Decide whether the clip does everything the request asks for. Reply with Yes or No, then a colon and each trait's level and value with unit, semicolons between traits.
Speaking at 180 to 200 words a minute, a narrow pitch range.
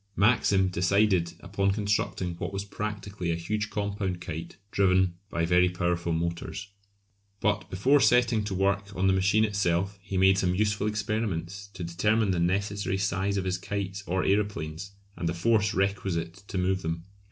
No: average, 165 wpm; narrow, 2.3 semitones